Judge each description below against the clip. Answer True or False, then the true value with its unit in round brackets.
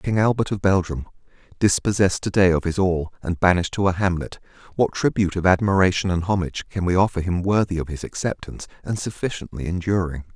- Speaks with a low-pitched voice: True (90 Hz)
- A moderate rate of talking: True (180 wpm)